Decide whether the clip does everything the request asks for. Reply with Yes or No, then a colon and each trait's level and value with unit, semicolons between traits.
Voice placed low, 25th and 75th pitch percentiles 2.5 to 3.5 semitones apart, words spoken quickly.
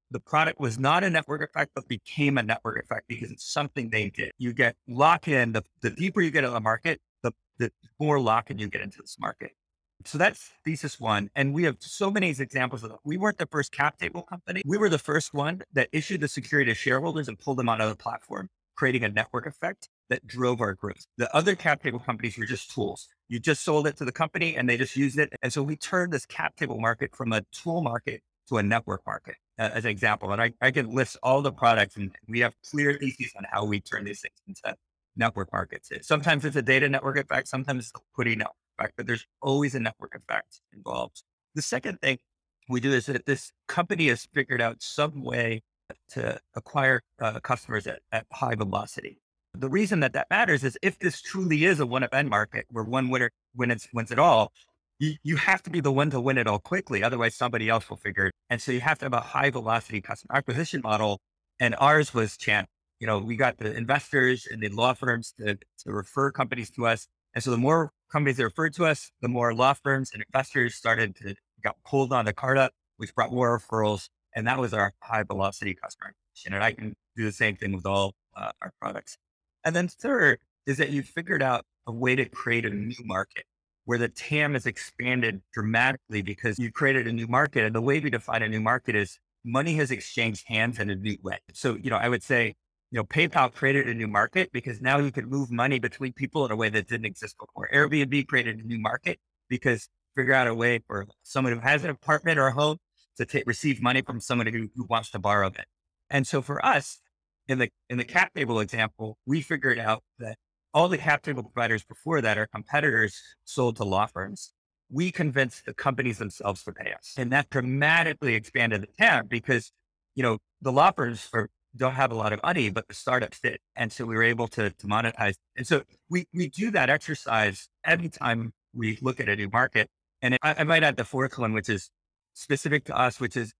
No: low, 125 Hz; average, 4.3 semitones; fast, 225 wpm